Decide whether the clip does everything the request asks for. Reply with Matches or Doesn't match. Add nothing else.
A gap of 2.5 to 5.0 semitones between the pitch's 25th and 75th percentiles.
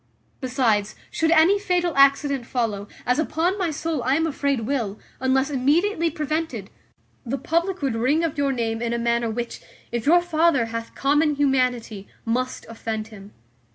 Doesn't match